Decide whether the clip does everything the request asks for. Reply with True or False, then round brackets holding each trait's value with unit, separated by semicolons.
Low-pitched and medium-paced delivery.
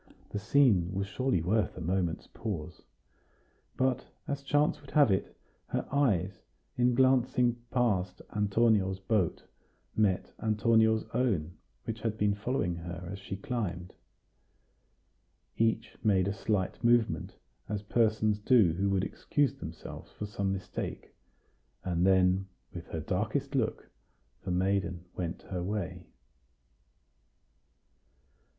False (100 Hz; 120 wpm)